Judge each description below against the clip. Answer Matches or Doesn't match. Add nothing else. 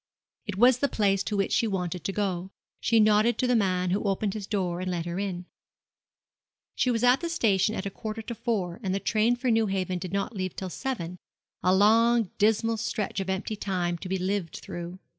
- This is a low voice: Doesn't match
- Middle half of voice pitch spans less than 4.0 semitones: Matches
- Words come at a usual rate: Doesn't match